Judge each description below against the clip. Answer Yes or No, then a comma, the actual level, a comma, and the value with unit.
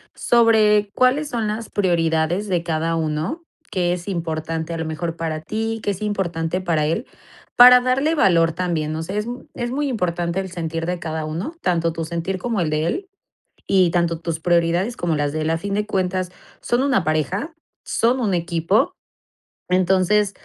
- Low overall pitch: No, medium, 180 Hz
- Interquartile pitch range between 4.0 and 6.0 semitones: Yes, average, 4.3 semitones